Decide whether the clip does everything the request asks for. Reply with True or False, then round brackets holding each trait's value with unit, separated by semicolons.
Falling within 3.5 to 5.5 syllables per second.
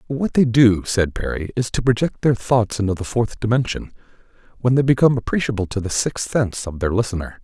False (5.8 syllables/s)